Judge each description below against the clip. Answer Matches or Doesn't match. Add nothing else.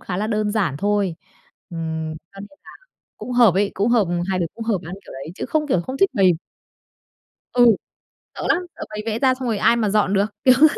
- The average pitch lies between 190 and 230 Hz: Matches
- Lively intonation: Doesn't match